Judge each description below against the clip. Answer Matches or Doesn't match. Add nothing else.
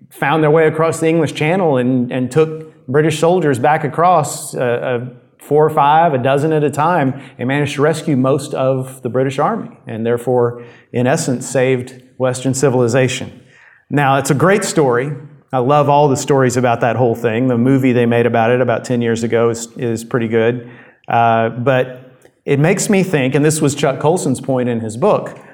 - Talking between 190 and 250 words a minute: Matches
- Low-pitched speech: Matches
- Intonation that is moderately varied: Matches